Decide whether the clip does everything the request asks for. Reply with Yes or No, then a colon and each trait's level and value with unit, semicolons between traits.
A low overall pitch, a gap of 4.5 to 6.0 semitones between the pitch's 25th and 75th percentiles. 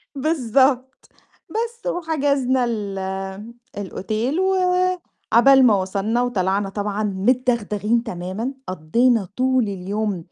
No: high, 235 Hz; average, 5.0 semitones